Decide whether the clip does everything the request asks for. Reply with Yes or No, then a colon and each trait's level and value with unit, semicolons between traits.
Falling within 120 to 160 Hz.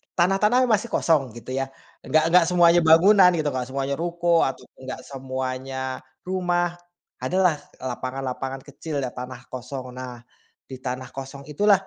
Yes: medium, 140 Hz